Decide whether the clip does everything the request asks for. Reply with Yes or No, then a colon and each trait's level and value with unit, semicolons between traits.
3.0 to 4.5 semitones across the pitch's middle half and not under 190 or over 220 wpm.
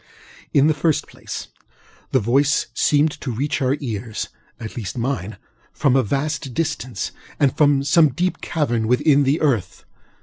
No: average, 3.8 semitones; average, 140 wpm